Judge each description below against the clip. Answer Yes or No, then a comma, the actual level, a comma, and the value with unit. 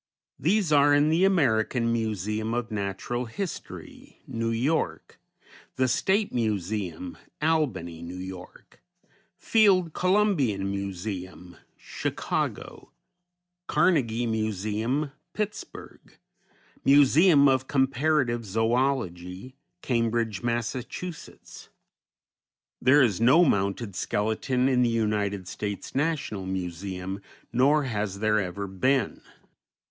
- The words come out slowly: Yes, slow, 90 wpm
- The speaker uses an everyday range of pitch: No, wide, 5.8 semitones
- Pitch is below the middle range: Yes, low, 115 Hz